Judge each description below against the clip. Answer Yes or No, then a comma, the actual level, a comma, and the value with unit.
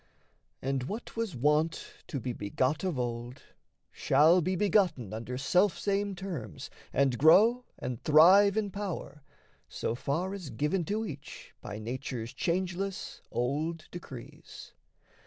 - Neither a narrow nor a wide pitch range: No, wide, 7.1 semitones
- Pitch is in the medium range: Yes, medium, 155 Hz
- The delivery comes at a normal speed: No, slow, 125 wpm